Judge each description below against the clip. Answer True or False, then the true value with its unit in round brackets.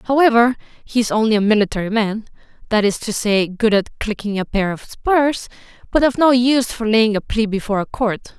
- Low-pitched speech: False (225 Hz)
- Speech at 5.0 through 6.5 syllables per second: True (5.5 syllables/s)